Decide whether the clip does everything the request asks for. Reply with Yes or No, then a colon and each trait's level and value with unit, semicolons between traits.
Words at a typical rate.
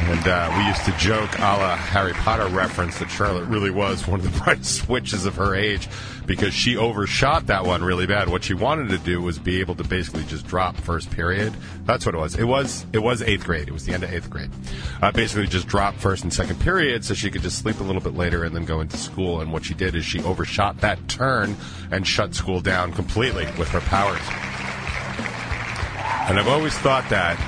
No: fast, 230 wpm